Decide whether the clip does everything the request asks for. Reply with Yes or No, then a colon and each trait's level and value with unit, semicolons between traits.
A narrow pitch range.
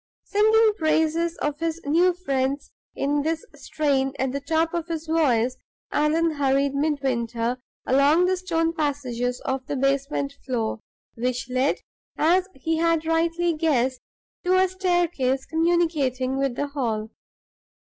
No: average, 3.9 semitones